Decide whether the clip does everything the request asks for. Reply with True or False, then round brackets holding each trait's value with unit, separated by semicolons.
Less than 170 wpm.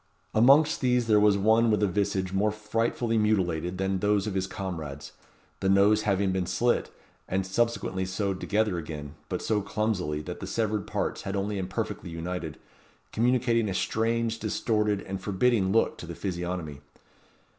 True (160 wpm)